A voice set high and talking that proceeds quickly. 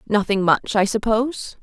No: high, 215 Hz; average, 150 wpm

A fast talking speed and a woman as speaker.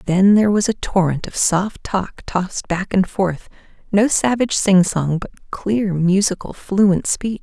No: average, 170 wpm; female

